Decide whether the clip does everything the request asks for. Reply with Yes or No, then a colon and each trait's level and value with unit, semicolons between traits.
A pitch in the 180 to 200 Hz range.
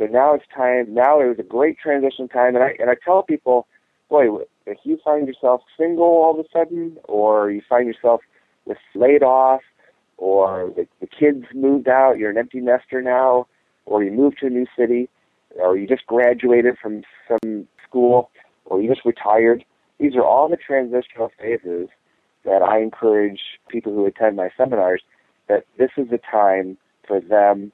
No: low, 125 Hz